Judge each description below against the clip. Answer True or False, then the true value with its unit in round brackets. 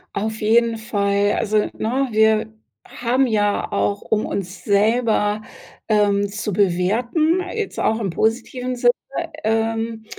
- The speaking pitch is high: True (220 Hz)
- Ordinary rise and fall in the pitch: False (2.3 semitones)